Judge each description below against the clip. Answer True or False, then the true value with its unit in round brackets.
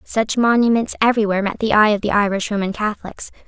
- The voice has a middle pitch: False (210 Hz)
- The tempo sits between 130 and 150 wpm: False (205 wpm)